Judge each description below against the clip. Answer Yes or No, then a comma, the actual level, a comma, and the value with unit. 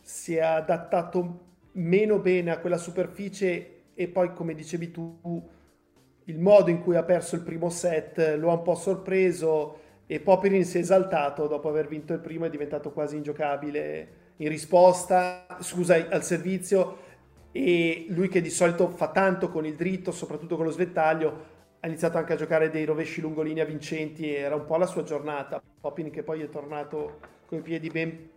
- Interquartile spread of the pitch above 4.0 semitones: No, narrow, 2.5 semitones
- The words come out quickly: Yes, fast, 180 wpm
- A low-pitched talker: No, medium, 165 Hz